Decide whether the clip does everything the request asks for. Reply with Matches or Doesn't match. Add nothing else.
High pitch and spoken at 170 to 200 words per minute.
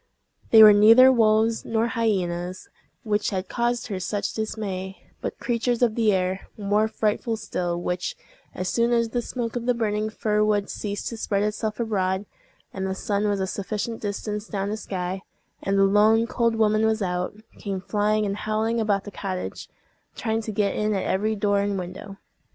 Matches